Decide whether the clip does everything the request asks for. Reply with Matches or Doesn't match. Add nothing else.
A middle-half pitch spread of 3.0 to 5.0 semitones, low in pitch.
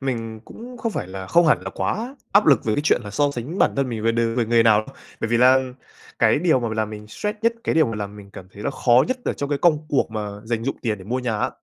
Doesn't match